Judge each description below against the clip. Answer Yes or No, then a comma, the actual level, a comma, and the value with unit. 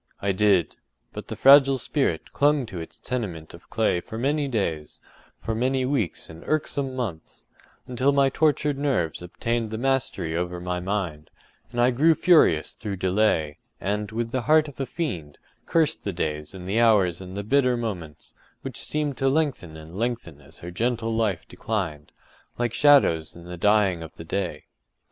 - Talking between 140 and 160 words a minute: No, average, 170 wpm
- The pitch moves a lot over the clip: Yes, wide, 7.3 semitones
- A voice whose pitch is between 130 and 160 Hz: No, low, 110 Hz